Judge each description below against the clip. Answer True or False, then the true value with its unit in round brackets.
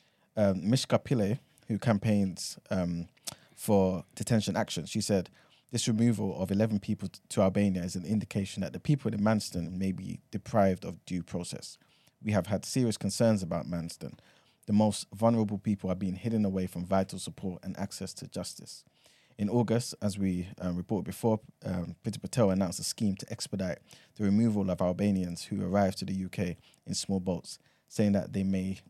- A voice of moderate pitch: False (100 Hz)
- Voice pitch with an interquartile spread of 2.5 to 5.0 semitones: True (2.8 semitones)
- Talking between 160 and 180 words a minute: True (175 wpm)